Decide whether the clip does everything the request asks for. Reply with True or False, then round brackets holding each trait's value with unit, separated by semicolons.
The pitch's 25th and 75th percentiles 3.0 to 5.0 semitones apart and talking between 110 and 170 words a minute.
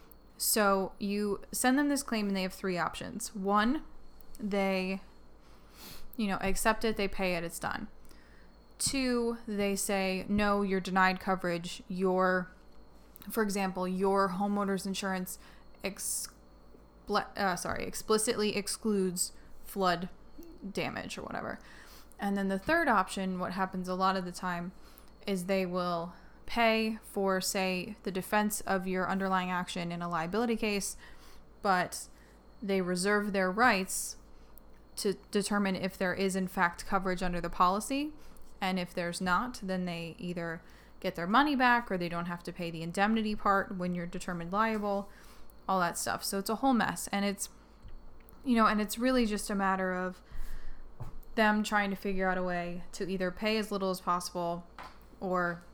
False (2.5 semitones; 155 wpm)